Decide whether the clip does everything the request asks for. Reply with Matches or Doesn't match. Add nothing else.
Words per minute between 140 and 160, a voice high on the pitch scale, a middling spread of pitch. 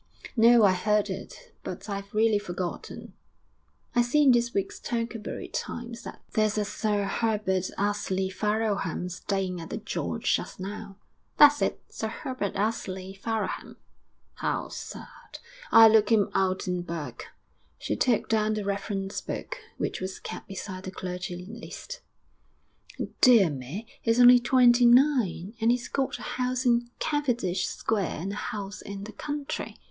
Matches